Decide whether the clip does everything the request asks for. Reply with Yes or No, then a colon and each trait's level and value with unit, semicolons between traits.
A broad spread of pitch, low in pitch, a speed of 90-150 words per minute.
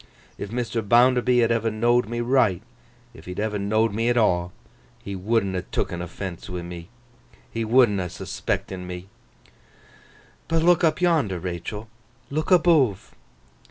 No: average, 4.5 semitones; low, 110 Hz; average, 140 wpm